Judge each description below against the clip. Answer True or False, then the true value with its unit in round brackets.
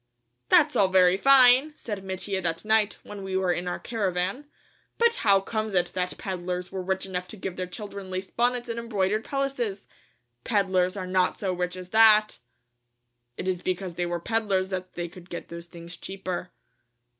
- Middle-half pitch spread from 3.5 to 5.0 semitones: False (3.0 semitones)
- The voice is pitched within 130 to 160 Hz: False (190 Hz)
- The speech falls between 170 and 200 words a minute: True (180 wpm)